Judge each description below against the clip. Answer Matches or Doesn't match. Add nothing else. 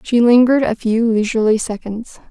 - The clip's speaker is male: Doesn't match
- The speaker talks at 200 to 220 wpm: Doesn't match